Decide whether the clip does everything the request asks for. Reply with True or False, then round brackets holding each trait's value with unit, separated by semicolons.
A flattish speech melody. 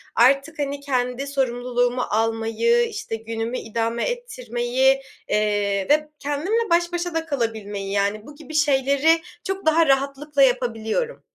False (5.4 semitones)